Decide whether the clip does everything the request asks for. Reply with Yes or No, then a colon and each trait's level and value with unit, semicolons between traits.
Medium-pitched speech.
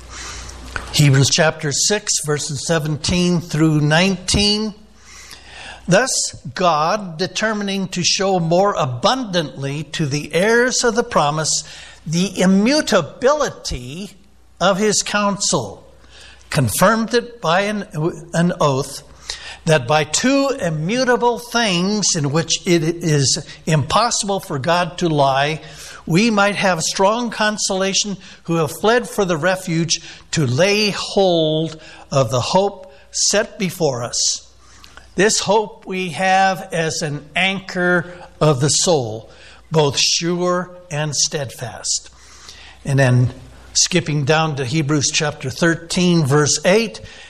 Yes: medium, 175 Hz